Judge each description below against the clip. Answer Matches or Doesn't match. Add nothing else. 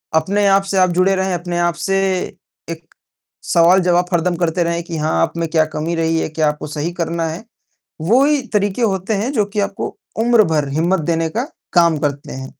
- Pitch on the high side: Doesn't match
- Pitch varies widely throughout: Doesn't match